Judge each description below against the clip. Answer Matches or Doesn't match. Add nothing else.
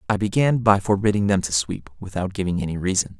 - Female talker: Doesn't match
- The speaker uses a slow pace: Doesn't match